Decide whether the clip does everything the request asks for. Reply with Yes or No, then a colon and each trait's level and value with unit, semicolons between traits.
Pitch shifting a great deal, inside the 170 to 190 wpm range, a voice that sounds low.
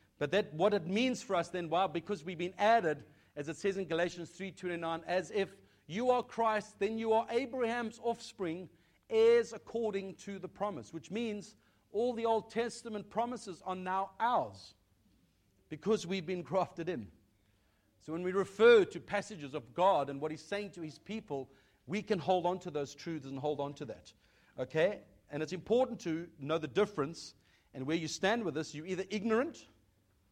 No: wide, 5.7 semitones; average, 185 wpm; medium, 185 Hz